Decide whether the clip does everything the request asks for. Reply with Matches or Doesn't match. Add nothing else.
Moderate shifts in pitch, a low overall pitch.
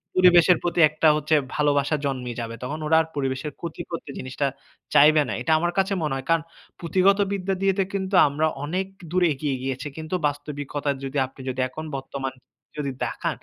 Doesn't match